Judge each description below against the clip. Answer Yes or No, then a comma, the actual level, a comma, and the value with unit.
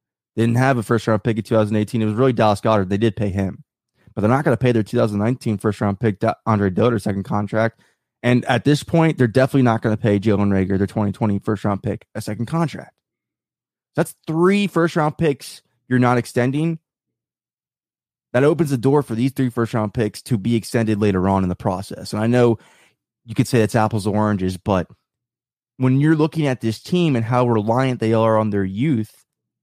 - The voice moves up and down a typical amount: Yes, average, 3.4 semitones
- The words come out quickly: Yes, fast, 210 wpm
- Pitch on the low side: Yes, low, 115 Hz